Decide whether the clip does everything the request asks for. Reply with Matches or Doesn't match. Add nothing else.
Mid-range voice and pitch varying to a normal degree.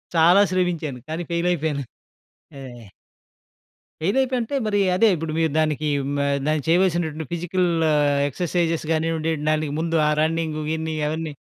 Doesn't match